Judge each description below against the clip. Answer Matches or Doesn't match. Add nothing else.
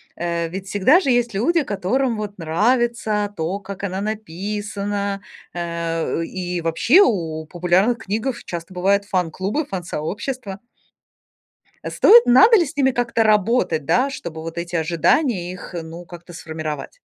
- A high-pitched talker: Matches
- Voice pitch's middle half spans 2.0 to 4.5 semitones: Doesn't match